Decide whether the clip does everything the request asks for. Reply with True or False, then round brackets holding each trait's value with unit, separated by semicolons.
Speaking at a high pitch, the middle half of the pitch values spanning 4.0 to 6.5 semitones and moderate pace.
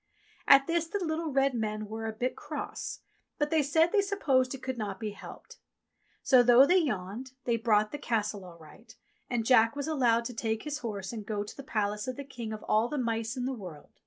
False (240 Hz; 4.4 semitones; 230 wpm)